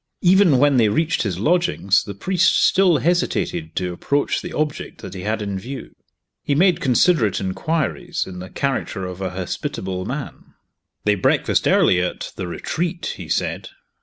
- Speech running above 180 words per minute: No, average, 165 wpm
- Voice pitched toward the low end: Yes, low, 130 Hz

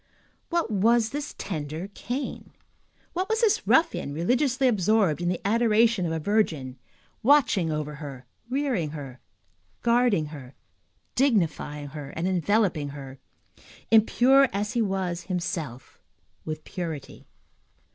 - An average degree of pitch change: No, wide, 7.7 semitones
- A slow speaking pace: Yes, slow, 120 wpm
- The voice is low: No, medium, 185 Hz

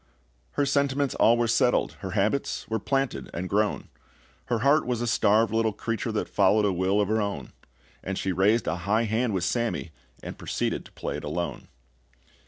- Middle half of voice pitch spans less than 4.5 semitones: Yes, average, 3.4 semitones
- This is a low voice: Yes, low, 110 Hz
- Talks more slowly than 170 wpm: No, average, 190 wpm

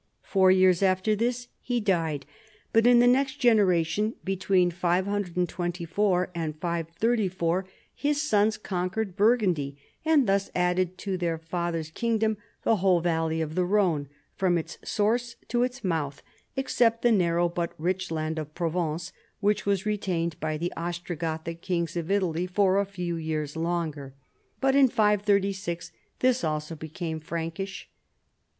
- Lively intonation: No, average, 3.9 semitones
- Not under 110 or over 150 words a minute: Yes, average, 145 wpm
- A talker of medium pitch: Yes, medium, 180 Hz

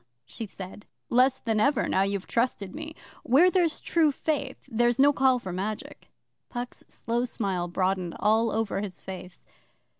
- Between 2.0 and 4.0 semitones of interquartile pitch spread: No, wide, 5.4 semitones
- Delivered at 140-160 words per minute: Yes, average, 155 wpm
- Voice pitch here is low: No, high, 225 Hz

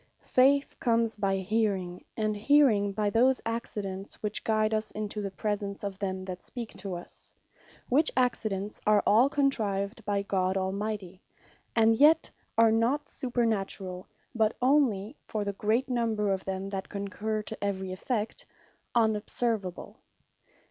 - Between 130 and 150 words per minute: Yes, average, 140 wpm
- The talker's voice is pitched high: Yes, high, 210 Hz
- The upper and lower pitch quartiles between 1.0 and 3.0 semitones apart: Yes, average, 2.7 semitones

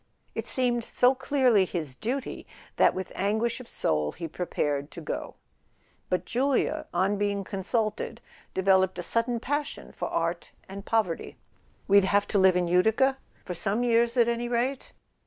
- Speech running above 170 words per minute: No, average, 155 wpm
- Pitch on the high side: Yes, high, 205 Hz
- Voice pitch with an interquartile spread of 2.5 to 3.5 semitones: No, average, 4.5 semitones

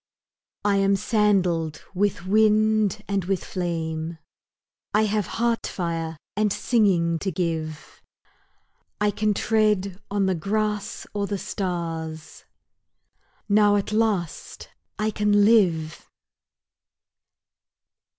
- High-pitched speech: Yes, high, 200 Hz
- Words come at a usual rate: No, slow, 100 wpm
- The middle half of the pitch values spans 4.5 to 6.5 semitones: No, average, 3.8 semitones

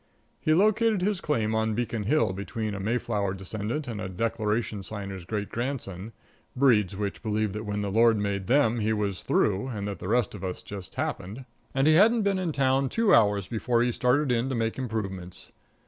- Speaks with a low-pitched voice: Yes, low, 110 Hz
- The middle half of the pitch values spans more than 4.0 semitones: Yes, average, 4.4 semitones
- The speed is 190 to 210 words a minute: Yes, average, 195 wpm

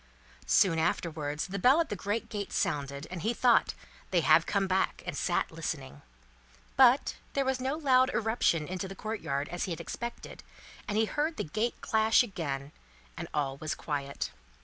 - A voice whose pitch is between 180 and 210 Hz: Yes, high, 190 Hz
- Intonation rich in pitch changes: Yes, wide, 7.1 semitones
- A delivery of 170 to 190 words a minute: Yes, average, 175 wpm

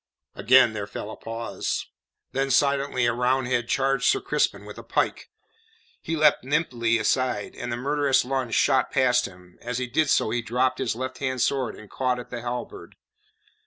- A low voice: Yes, low, 125 Hz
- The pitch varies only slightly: Yes, narrow, 2.2 semitones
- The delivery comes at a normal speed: Yes, average, 180 wpm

